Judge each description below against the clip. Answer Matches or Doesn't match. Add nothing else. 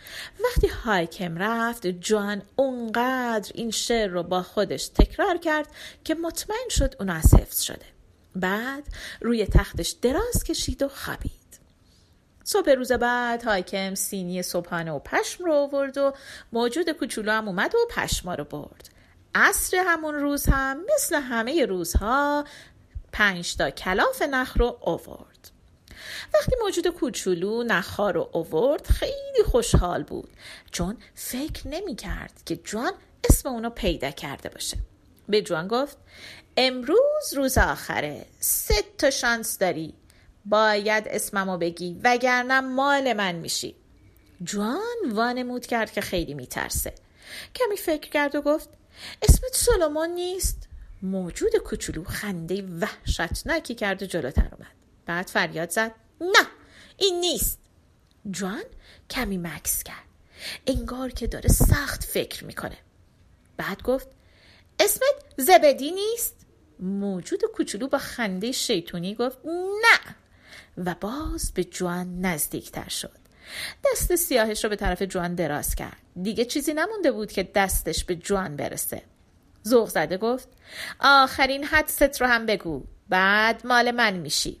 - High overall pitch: Matches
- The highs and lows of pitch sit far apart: Matches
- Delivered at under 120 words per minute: Doesn't match